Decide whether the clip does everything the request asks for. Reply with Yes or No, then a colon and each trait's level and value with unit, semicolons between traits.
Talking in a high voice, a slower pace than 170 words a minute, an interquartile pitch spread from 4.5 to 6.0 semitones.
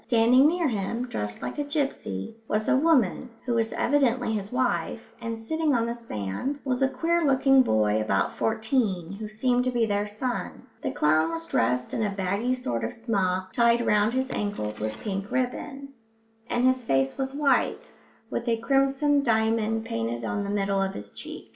No: high, 225 Hz; average, 185 wpm; average, 5.0 semitones